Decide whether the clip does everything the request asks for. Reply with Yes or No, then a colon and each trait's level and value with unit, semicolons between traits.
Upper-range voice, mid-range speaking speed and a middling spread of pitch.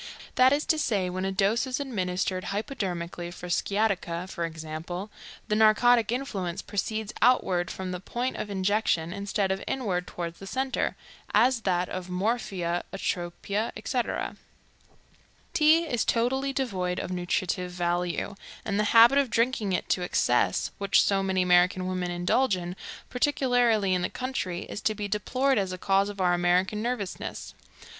Yes: high, 195 Hz; average, 160 wpm; average, 4.4 semitones